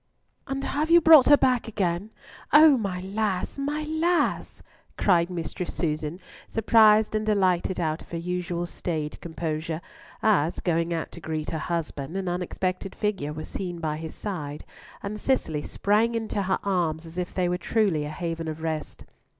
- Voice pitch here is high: No, medium, 180 Hz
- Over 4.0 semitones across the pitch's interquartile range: Yes, average, 4.7 semitones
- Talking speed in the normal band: Yes, average, 165 wpm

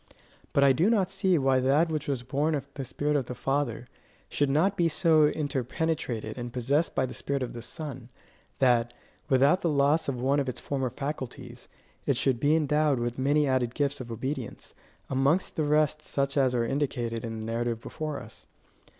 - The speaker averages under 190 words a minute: No, average, 195 wpm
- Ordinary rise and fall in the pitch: Yes, average, 3.3 semitones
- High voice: No, medium, 140 Hz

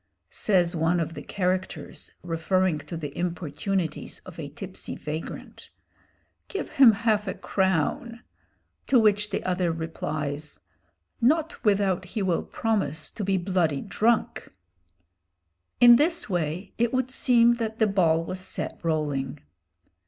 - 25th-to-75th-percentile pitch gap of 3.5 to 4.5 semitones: No, average, 5.1 semitones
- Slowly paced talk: Yes, slow, 130 wpm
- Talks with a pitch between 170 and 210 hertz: Yes, medium, 185 Hz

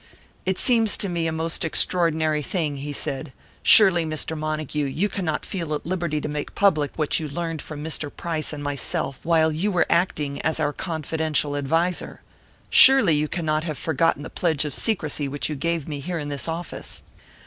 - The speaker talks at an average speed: Yes, average, 185 wpm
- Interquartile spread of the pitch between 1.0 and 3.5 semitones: Yes, narrow, 2.4 semitones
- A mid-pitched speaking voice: Yes, medium, 155 Hz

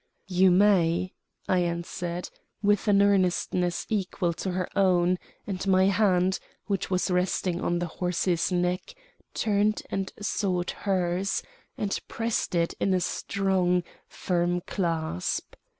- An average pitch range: No, narrow, 1.9 semitones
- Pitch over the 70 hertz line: Yes, medium, 185 Hz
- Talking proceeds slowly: Yes, slow, 125 wpm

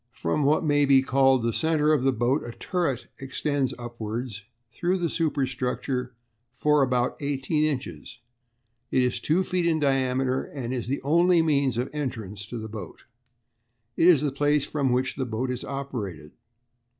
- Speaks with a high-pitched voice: No, low, 135 Hz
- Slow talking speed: No, average, 165 wpm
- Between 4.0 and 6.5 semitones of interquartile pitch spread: No, average, 3.3 semitones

